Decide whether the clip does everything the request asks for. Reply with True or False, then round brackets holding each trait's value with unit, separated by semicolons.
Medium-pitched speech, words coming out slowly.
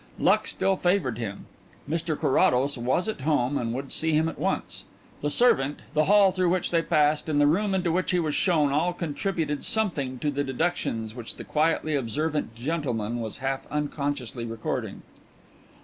False (150 Hz; 175 wpm)